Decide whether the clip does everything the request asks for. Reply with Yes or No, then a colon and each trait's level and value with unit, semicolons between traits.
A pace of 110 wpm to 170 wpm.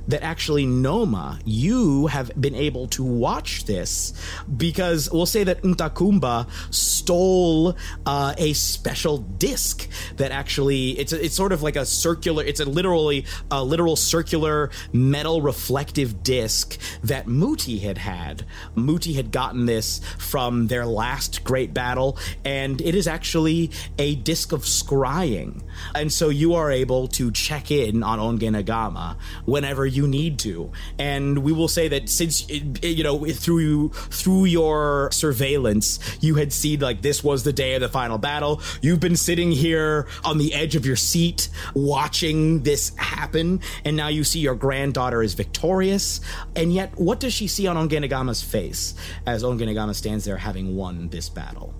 Yes: average, 160 wpm